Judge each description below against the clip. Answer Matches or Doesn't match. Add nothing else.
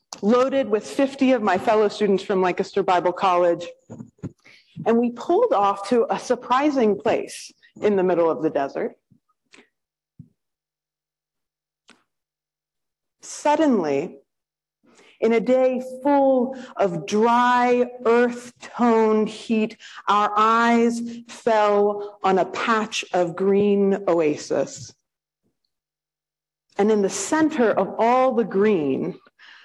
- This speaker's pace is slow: Matches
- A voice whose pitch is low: Doesn't match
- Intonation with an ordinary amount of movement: Matches